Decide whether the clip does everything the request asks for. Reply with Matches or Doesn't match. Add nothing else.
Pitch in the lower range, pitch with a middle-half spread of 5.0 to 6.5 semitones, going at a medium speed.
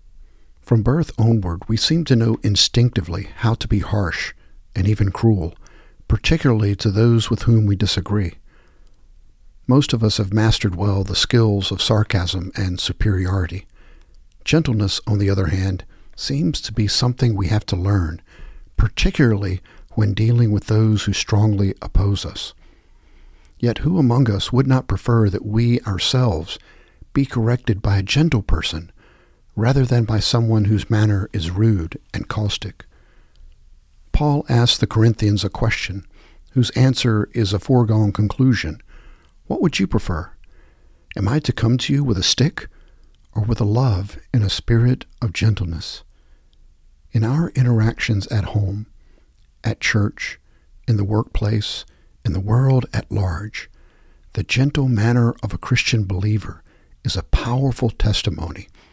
Doesn't match